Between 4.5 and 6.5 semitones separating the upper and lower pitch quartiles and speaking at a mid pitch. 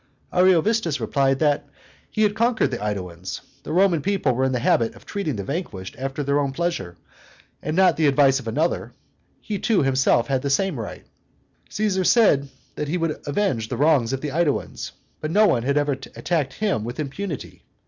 Yes: wide, 5.5 semitones; medium, 145 Hz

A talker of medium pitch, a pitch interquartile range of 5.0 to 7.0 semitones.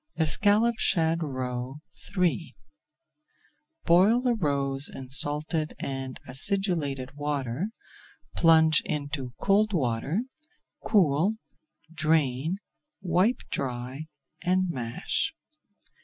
Yes: medium, 155 Hz; average, 5.3 semitones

